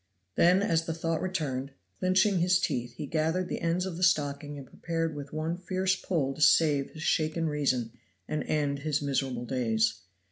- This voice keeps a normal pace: Yes, average, 180 wpm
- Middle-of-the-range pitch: Yes, medium, 155 Hz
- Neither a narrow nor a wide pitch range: Yes, average, 3.5 semitones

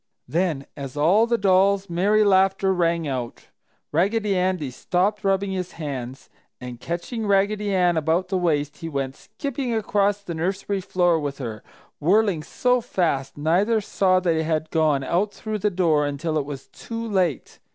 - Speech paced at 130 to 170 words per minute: Yes, average, 160 wpm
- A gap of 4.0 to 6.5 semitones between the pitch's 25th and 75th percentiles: Yes, average, 4.7 semitones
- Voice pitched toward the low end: No, medium, 180 Hz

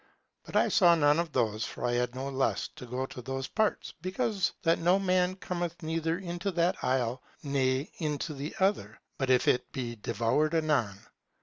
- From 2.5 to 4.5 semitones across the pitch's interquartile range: No, average, 5.3 semitones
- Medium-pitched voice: Yes, medium, 150 Hz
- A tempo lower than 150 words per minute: No, average, 185 wpm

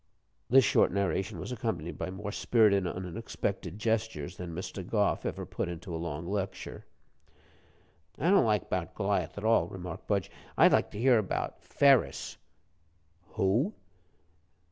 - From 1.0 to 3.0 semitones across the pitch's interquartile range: No, average, 3.6 semitones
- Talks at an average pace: Yes, average, 145 wpm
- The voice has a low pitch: Yes, low, 100 Hz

